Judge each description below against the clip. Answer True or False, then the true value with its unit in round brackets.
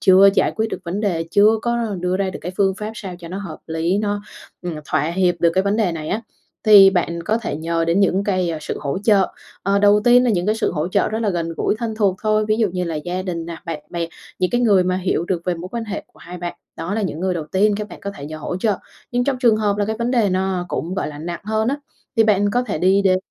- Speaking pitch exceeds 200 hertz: False (190 Hz)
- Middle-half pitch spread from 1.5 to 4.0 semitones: True (3.4 semitones)